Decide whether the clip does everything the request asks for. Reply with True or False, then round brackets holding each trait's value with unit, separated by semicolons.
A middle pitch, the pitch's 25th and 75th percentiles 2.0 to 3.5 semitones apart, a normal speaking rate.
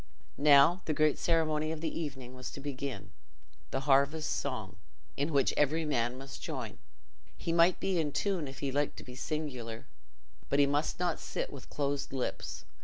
True (145 Hz; 2.8 semitones; 175 wpm)